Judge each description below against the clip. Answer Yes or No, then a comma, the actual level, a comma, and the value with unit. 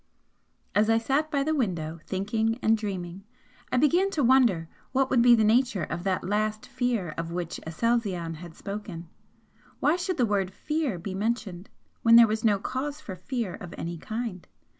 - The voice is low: No, high, 215 Hz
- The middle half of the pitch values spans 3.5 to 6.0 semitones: Yes, wide, 5.4 semitones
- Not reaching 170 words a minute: No, average, 180 wpm